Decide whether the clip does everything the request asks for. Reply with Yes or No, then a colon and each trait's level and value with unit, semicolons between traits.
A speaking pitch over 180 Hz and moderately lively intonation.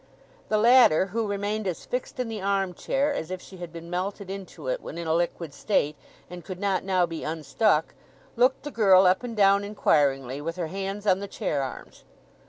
Yes: high, 190 Hz; average, 3.8 semitones